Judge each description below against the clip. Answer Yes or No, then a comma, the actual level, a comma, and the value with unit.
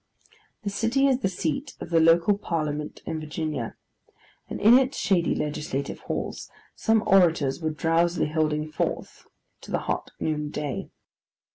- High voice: No, medium, 165 Hz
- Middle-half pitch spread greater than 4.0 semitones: Yes, average, 4.4 semitones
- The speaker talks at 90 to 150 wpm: Yes, average, 145 wpm